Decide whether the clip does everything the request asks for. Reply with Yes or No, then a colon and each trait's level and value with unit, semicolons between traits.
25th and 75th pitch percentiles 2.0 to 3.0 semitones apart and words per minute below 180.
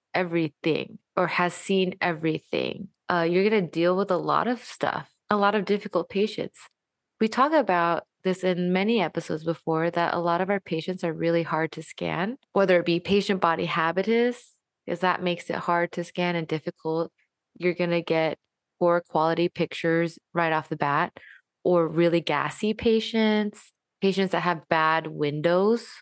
Yes: average, 2.7 semitones; average, 170 wpm